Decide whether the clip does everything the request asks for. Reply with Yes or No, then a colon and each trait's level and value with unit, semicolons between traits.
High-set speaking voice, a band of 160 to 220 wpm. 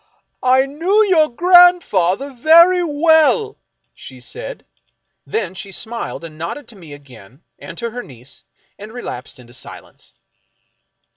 No: high, 245 Hz; slow, 135 wpm